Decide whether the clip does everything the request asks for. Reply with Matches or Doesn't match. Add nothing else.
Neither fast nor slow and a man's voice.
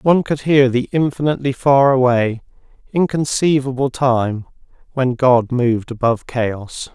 Doesn't match